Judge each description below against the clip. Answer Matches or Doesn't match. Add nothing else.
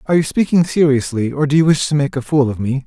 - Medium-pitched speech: Matches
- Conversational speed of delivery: Doesn't match